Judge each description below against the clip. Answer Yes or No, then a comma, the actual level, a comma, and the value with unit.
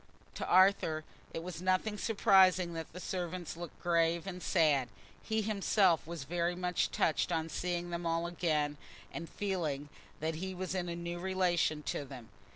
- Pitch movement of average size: No, narrow, 2.3 semitones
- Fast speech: No, average, 165 wpm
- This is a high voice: No, medium, 175 Hz